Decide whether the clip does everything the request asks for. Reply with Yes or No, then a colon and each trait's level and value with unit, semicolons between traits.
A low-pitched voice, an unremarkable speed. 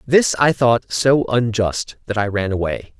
Yes: low, 115 Hz; average, 180 wpm